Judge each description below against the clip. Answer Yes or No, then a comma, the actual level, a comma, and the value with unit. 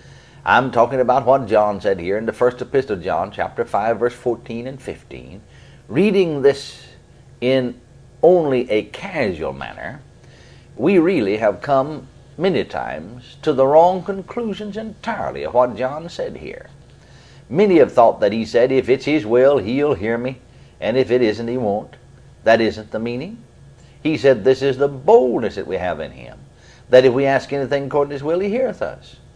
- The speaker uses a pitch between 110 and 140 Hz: Yes, low, 135 Hz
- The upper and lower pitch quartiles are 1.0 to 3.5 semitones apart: Yes, average, 2.7 semitones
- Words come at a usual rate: Yes, average, 180 wpm